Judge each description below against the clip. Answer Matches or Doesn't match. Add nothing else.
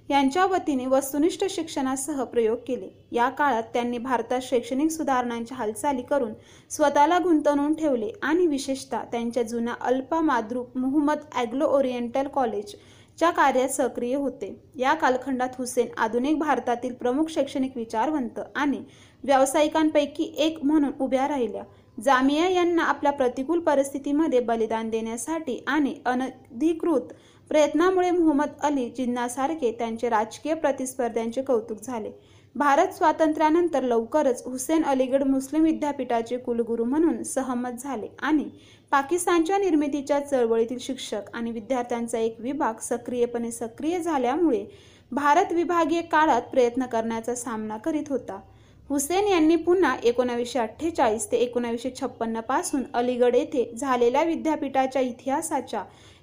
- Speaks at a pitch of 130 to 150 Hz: Doesn't match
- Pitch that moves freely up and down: Doesn't match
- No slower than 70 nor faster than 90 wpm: Doesn't match